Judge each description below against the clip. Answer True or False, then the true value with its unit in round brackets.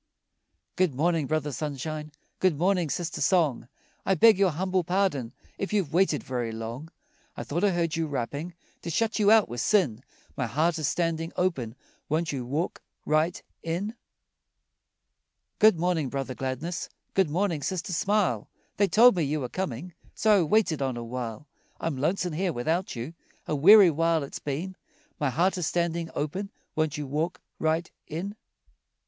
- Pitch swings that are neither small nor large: True (4.5 semitones)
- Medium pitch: True (165 Hz)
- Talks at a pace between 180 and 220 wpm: False (165 wpm)